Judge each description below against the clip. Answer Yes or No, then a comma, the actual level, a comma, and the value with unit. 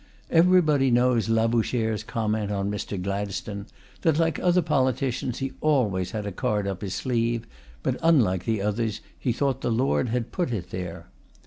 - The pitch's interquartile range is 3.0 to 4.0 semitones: No, average, 4.4 semitones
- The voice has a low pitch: Yes, low, 115 Hz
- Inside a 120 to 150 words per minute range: No, average, 160 wpm